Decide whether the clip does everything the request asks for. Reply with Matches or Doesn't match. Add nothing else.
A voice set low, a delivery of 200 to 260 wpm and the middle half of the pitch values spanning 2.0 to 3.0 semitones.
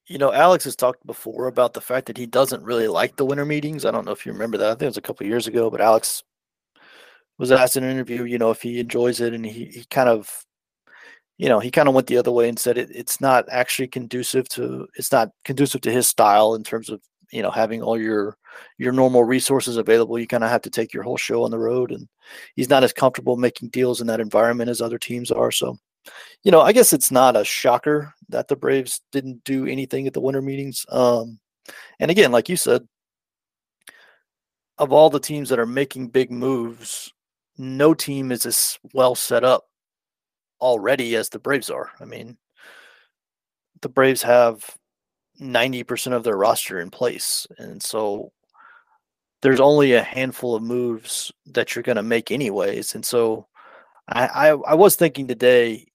Matches